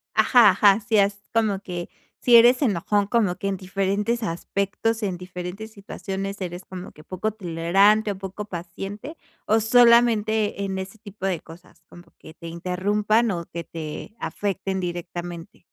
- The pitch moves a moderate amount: Yes, average, 3.2 semitones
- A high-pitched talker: Yes, high, 195 Hz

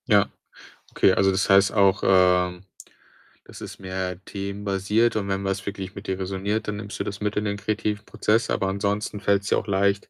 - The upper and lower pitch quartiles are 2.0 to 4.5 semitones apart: No, narrow, 1.3 semitones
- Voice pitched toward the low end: Yes, low, 100 Hz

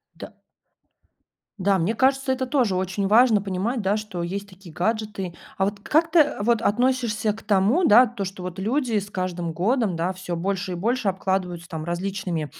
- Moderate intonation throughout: Yes, average, 3.9 semitones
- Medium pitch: No, high, 200 Hz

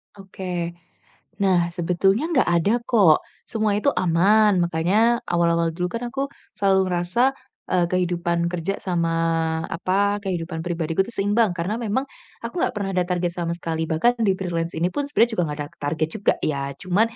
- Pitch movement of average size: Yes, average, 3.4 semitones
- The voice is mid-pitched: Yes, medium, 180 Hz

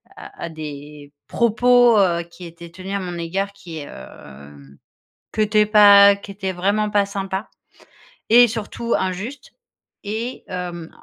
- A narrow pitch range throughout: No, average, 3.9 semitones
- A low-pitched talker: No, high, 195 Hz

